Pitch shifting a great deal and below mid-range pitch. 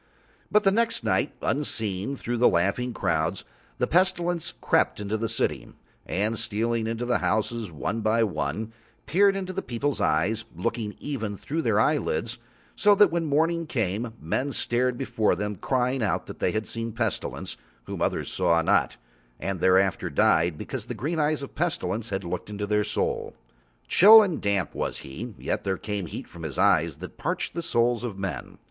Yes: wide, 6.5 semitones; low, 115 Hz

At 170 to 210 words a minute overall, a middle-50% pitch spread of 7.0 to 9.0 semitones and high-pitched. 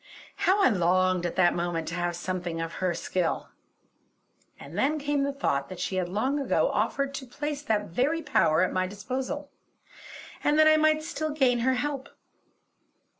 Yes: average, 175 wpm; wide, 8.4 semitones; high, 245 Hz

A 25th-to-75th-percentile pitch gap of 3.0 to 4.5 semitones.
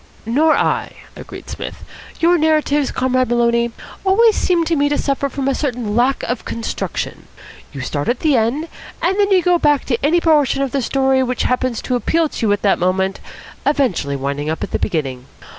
No: average, 5.1 semitones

